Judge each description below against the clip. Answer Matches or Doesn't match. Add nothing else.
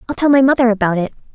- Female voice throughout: Matches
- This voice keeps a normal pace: Doesn't match